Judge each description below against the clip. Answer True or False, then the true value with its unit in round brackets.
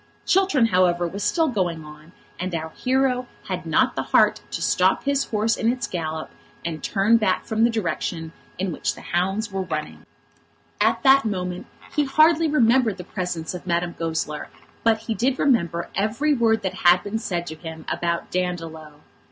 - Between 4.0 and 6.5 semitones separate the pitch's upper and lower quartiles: True (5.5 semitones)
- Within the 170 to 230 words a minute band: True (175 wpm)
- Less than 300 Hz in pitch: True (190 Hz)